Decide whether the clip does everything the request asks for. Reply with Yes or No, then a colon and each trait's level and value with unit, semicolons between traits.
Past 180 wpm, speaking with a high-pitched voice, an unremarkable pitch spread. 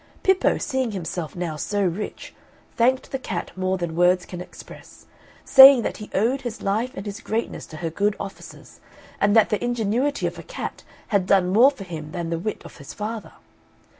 Yes: average, 195 wpm; high, 205 Hz; average, 4.7 semitones